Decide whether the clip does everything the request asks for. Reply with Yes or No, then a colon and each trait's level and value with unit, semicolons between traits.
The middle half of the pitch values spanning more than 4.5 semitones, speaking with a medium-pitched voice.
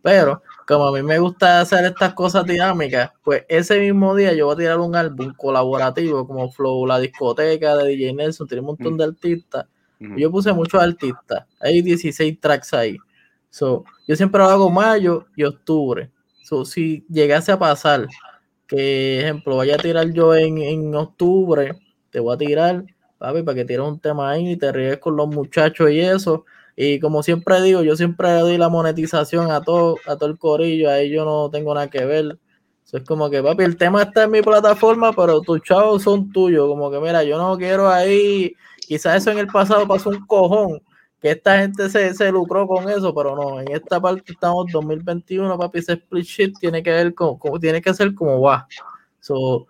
No: average, 3.9 semitones; medium, 165 Hz